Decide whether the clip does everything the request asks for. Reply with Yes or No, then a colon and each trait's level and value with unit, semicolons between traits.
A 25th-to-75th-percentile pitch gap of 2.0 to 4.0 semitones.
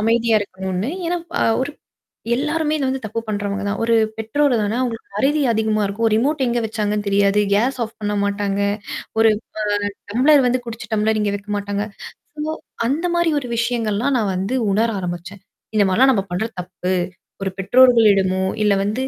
Yes: average, 3.6 semitones